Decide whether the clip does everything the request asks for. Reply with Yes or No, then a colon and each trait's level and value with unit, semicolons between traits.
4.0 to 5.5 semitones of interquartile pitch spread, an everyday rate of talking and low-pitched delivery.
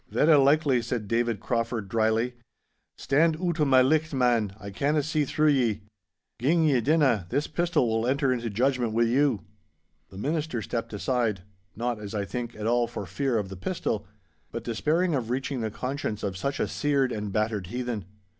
Yes: average, 4.4 semitones; average, 180 wpm; low, 120 Hz